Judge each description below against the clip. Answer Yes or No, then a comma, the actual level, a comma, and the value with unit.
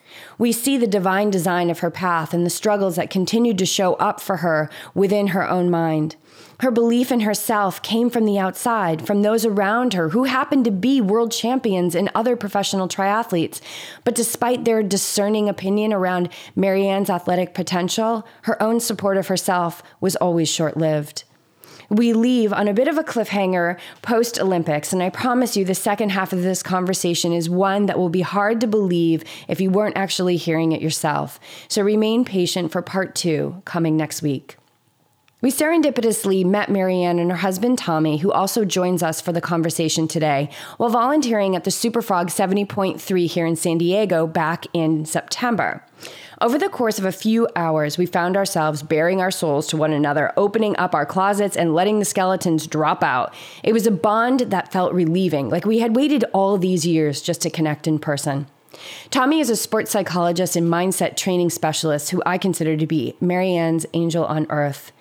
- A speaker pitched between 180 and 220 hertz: Yes, medium, 185 Hz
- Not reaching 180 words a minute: No, average, 185 wpm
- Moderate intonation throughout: Yes, average, 4.1 semitones